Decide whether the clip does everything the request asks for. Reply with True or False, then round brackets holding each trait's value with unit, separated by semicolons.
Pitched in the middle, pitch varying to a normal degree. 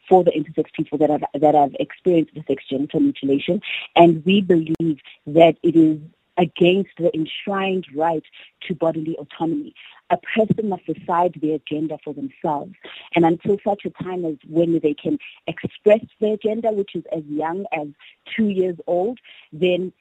True (165 Hz; 3.1 semitones)